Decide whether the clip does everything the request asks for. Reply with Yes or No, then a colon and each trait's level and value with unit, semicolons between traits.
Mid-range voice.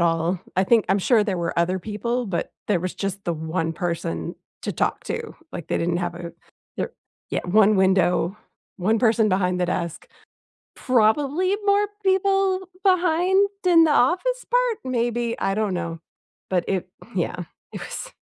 No: high, 200 Hz